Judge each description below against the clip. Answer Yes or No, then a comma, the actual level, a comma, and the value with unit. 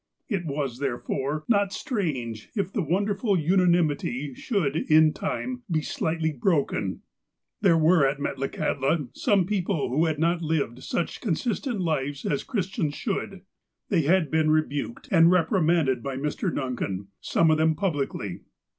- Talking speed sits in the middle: Yes, average, 150 wpm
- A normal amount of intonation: Yes, average, 5.0 semitones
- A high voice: No, medium, 160 Hz